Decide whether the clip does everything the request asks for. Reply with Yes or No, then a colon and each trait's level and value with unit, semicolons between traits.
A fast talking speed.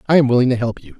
Yes: fast, 365 wpm